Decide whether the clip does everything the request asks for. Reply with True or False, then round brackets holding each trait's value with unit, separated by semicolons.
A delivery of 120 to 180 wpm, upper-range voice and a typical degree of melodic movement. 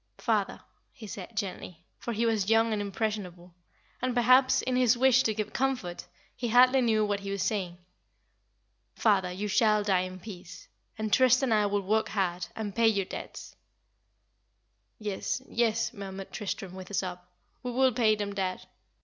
True (170 wpm; 210 Hz; 3.5 semitones)